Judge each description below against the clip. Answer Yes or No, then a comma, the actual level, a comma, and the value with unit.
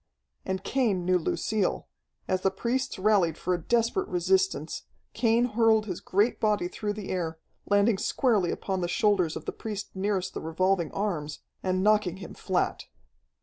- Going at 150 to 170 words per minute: Yes, average, 160 wpm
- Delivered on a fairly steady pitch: No, average, 3.0 semitones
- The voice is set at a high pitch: Yes, high, 195 Hz